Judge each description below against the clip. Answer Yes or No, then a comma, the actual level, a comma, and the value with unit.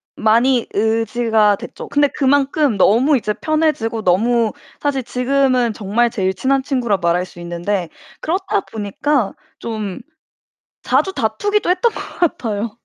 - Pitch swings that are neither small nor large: Yes, average, 5.0 semitones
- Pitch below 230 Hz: No, high, 235 Hz